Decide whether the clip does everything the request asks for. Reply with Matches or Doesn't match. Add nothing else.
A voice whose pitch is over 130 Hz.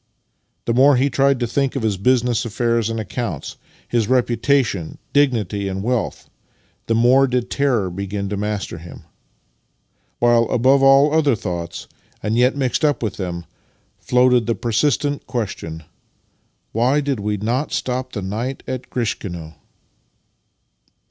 Doesn't match